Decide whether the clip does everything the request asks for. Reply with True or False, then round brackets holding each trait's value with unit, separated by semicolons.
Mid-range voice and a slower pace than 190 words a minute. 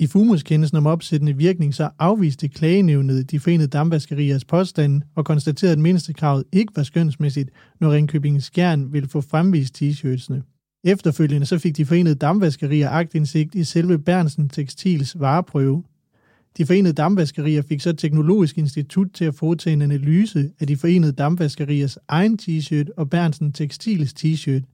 True (155 Hz; 145 wpm)